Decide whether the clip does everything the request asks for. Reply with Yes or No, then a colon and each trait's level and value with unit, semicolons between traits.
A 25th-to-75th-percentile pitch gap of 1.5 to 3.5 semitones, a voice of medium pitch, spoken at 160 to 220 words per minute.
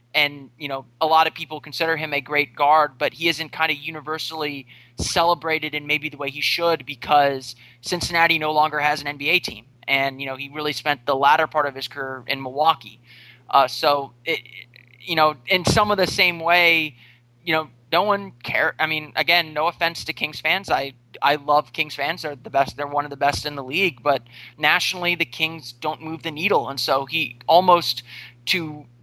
Yes: average, 3.2 semitones; medium, 150 Hz; fast, 205 wpm